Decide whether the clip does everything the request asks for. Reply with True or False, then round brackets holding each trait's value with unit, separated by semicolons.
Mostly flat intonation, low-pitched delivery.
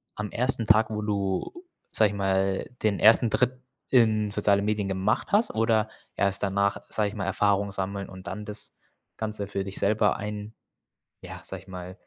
True (1.8 semitones; 105 Hz)